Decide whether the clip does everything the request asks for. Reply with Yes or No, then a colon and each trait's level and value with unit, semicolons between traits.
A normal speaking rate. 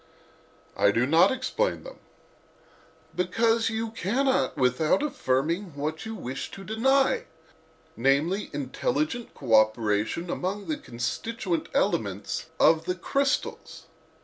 No: slow, 105 wpm